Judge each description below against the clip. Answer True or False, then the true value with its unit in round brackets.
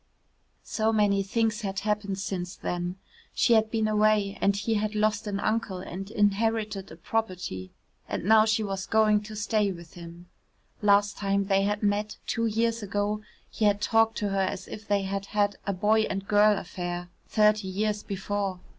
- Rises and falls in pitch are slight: True (1.7 semitones)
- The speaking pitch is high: True (205 Hz)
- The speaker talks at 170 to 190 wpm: True (180 wpm)